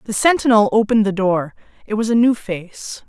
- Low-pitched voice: No, high, 215 Hz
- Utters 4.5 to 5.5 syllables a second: Yes, 5.4 syllables/s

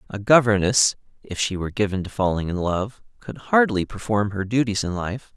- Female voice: No, male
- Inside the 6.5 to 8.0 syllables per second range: No, 5.3 syllables/s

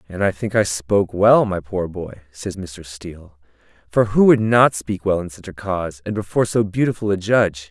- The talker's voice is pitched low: Yes, very low, 95 Hz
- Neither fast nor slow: No, fast, 220 wpm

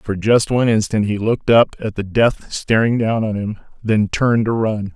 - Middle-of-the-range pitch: No, low, 110 Hz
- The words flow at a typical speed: No, fast, 220 wpm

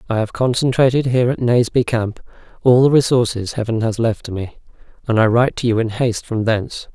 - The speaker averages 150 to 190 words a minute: No, average, 200 wpm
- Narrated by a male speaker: Yes, male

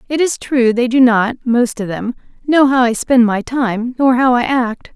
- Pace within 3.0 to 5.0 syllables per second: Yes, 4.4 syllables/s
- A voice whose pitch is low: No, high, 245 Hz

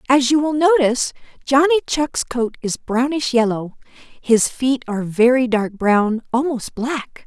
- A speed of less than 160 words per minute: Yes, average, 150 wpm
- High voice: Yes, very high, 255 Hz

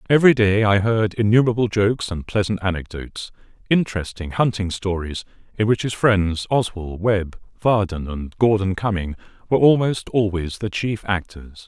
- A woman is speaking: No, male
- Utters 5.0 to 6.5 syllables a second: Yes, 5.1 syllables/s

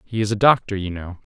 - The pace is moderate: No, fast, 265 wpm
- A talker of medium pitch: No, low, 105 Hz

